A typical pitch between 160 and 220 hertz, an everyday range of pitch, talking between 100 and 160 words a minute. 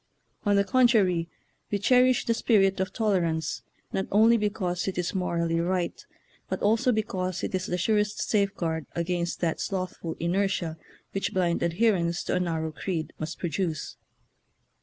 Yes: medium, 185 Hz; average, 3.3 semitones; average, 150 wpm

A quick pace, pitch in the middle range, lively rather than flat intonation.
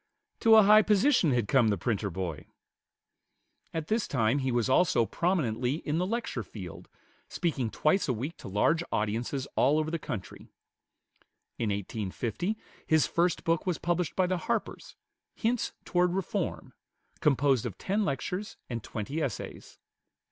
No: average, 150 wpm; medium, 150 Hz; wide, 7.4 semitones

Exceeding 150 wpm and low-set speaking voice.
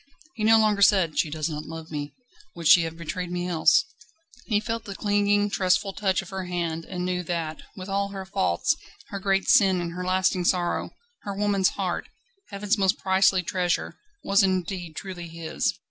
No: average, 185 wpm; medium, 185 Hz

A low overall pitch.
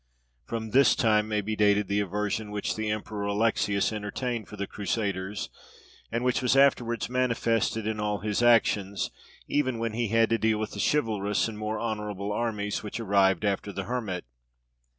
Yes: low, 105 Hz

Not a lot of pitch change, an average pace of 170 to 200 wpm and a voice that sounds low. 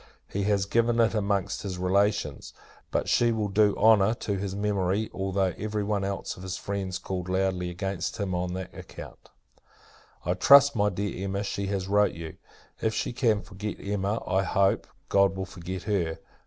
Yes: narrow, 1.8 semitones; average, 180 wpm; low, 100 Hz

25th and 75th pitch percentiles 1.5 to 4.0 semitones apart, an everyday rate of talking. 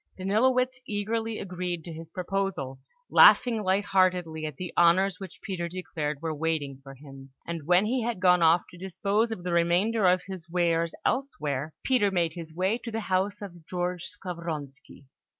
Yes: average, 3.3 semitones; average, 170 wpm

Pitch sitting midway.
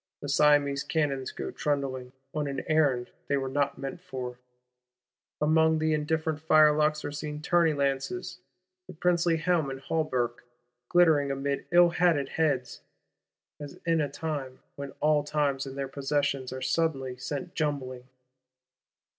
Yes: medium, 145 Hz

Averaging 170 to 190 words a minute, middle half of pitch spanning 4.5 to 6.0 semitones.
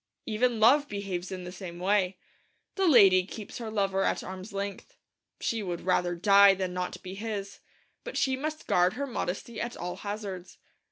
No: average, 175 wpm; average, 3.5 semitones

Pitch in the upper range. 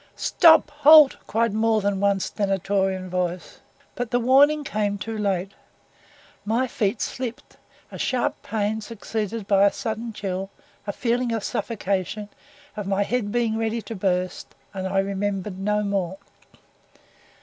Yes: high, 210 Hz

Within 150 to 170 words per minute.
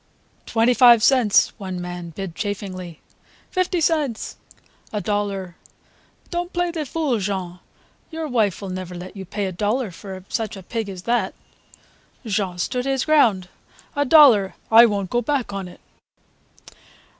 Yes: average, 155 wpm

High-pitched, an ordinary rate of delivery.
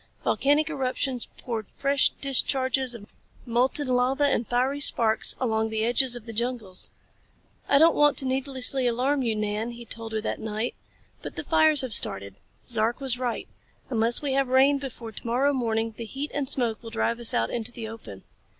Yes: high, 245 Hz; average, 185 wpm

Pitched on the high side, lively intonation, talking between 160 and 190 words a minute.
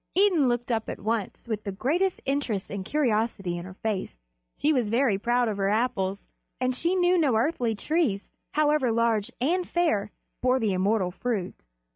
Yes: high, 235 Hz; wide, 5.7 semitones; average, 175 wpm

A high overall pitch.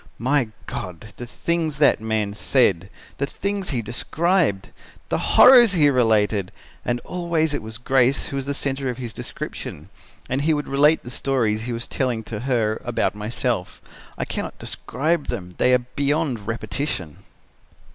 No: low, 125 Hz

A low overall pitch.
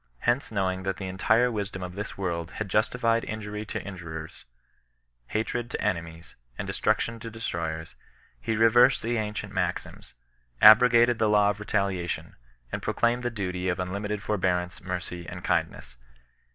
Yes: low, 100 Hz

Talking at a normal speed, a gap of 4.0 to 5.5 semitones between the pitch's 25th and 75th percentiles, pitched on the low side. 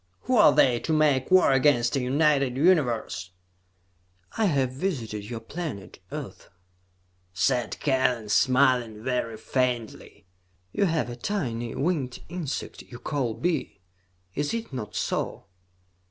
No: slow, 125 wpm; average, 4.4 semitones; low, 130 Hz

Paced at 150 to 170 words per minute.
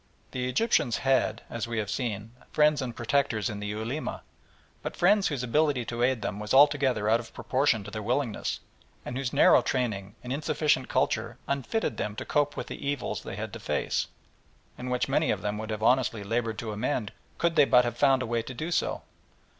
No: fast, 205 wpm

